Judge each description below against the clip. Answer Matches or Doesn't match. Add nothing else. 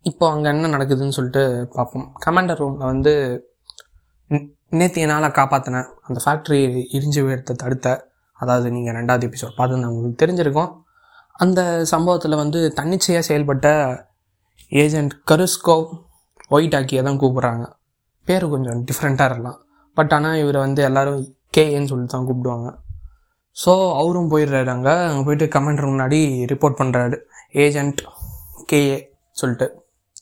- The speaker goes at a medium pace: Matches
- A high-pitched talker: Doesn't match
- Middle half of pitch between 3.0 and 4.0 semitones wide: Matches